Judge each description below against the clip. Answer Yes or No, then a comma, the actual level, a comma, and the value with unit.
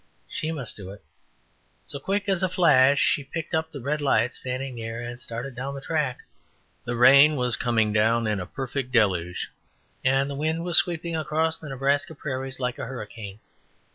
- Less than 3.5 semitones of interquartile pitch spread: No, average, 4.4 semitones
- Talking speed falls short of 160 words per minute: No, average, 185 wpm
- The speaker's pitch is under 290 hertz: Yes, low, 135 Hz